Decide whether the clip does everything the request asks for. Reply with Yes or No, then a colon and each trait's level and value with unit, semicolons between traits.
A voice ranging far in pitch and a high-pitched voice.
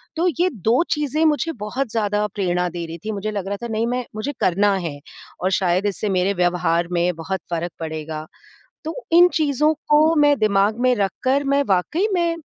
Yes: wide, 8.0 semitones; high, 210 Hz